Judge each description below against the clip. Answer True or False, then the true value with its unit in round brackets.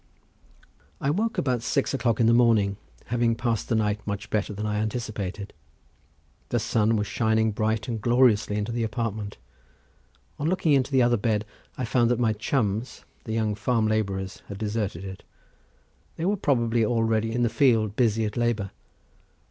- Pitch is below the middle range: True (110 Hz)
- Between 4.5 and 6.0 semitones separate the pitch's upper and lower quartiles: False (2.4 semitones)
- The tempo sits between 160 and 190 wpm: True (170 wpm)